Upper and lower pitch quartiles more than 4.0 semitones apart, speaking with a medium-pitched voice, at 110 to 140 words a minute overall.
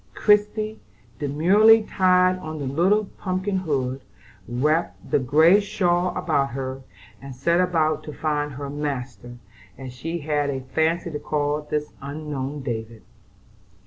Yes: average, 4.6 semitones; medium, 150 Hz; slow, 135 wpm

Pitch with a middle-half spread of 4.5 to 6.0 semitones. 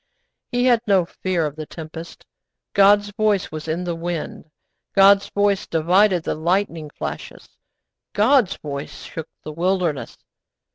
No: average, 3.9 semitones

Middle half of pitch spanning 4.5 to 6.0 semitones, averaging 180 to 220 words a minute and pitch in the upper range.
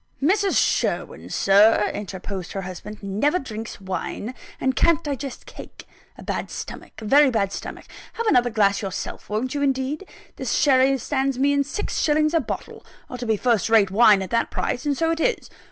Yes: wide, 5.5 semitones; average, 185 wpm; very high, 250 Hz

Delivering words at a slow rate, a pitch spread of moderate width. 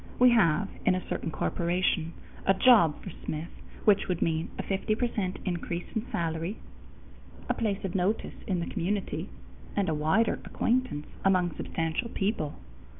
No: average, 150 wpm; average, 4.0 semitones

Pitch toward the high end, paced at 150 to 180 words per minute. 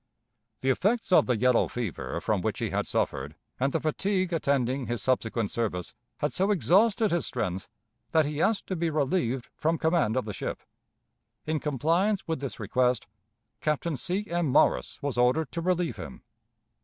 No: medium, 150 Hz; average, 170 wpm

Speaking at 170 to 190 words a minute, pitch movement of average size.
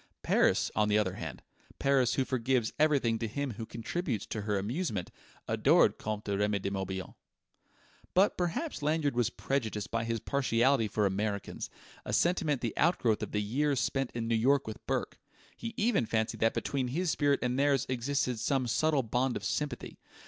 Yes: average, 175 wpm; average, 4.6 semitones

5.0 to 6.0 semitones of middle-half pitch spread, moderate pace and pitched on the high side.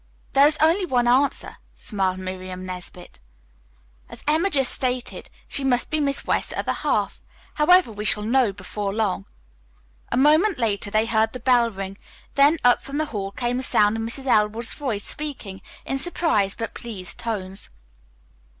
Yes: wide, 5.5 semitones; average, 165 wpm; high, 235 Hz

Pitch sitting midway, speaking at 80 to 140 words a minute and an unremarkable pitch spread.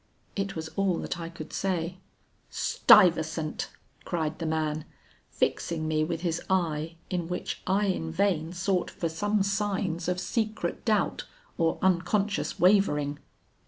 Yes: medium, 175 Hz; slow, 135 wpm; average, 3.3 semitones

